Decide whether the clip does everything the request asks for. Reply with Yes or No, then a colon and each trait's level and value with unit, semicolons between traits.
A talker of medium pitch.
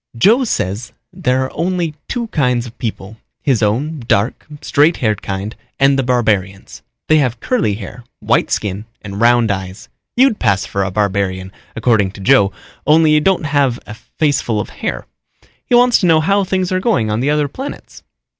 No: low, 125 Hz